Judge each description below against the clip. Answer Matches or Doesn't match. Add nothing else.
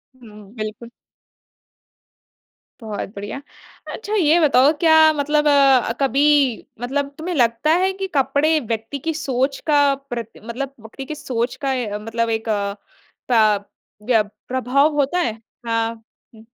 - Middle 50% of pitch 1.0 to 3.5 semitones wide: Doesn't match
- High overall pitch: Matches